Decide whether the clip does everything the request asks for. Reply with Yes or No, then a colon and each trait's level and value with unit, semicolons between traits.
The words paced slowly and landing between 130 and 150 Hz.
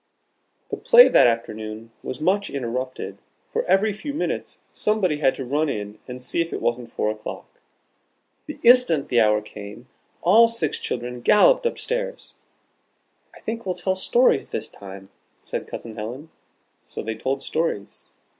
No: average, 155 wpm; medium, 140 Hz